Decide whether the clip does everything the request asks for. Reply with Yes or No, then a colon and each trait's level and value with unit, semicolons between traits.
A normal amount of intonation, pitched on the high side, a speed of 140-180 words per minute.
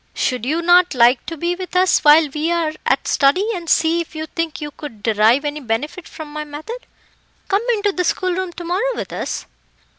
No: average, 3.4 semitones; very high, 320 Hz; fast, 205 wpm